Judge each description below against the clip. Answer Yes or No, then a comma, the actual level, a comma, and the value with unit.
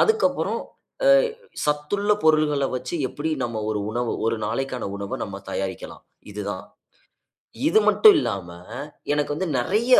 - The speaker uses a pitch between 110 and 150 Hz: Yes, low, 135 Hz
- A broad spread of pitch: Yes, wide, 6.9 semitones